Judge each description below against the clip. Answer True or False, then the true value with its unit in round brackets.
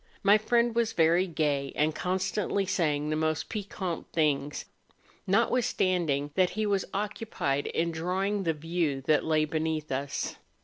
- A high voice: False (165 Hz)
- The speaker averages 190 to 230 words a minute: False (140 wpm)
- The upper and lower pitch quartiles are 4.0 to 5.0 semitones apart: True (4.4 semitones)